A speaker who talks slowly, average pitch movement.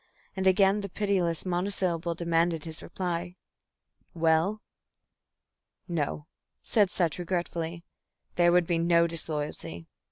No: slow, 105 wpm; narrow, 1.9 semitones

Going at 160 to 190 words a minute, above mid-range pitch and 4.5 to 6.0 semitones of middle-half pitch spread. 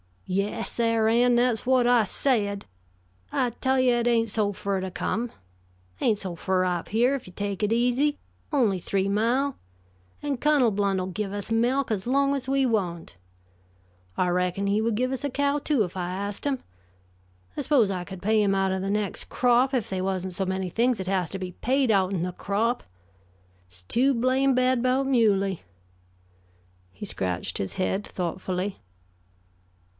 Yes: average, 180 wpm; high, 215 Hz; average, 4.9 semitones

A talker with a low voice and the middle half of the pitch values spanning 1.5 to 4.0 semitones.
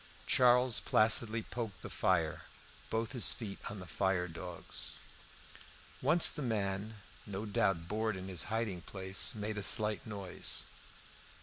Yes: low, 105 Hz; average, 2.9 semitones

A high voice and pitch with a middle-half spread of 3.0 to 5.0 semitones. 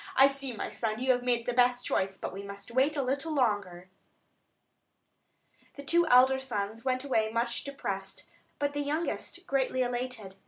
Yes: very high, 250 Hz; average, 4.0 semitones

